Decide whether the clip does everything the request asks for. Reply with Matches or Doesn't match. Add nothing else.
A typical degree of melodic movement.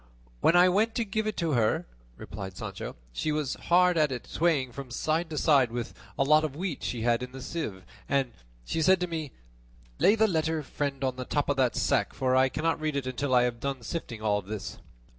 Matches